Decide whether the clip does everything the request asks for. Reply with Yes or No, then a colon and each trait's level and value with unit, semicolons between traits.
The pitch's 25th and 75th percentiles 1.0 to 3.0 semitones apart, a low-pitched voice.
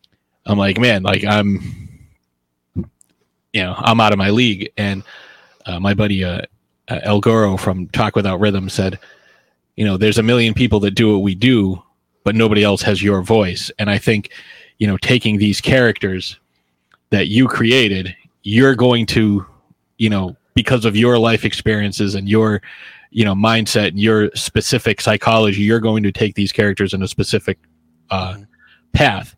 Yes: narrow, 2.6 semitones; low, 105 Hz